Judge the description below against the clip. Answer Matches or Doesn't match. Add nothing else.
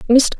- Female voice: Matches